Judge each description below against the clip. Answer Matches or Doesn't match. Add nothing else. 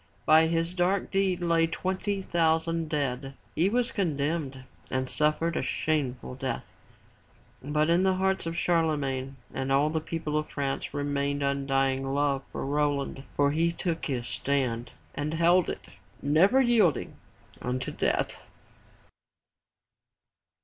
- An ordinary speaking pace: Doesn't match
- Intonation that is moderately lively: Matches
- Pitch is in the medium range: Matches